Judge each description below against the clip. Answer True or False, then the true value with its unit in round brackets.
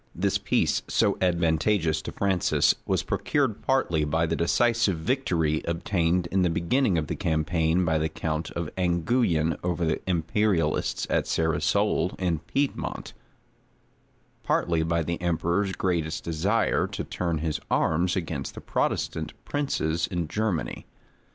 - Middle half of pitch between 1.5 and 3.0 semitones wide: True (2.5 semitones)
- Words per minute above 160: False (135 wpm)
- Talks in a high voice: False (85 Hz)